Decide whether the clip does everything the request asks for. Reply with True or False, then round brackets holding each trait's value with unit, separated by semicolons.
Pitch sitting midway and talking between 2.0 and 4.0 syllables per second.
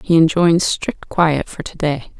True (165 Hz; 3.9 syllables/s)